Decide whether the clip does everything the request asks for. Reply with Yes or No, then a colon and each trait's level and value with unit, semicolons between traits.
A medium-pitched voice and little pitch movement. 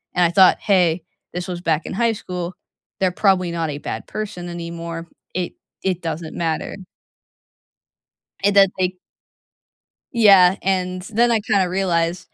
Yes: medium, 180 Hz; narrow, 2.3 semitones